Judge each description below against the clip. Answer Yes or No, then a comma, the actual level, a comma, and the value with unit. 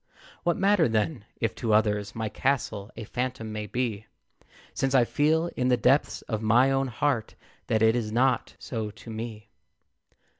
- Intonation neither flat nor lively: Yes, average, 3.5 semitones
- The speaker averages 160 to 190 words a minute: Yes, average, 165 wpm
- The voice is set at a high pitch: No, low, 115 Hz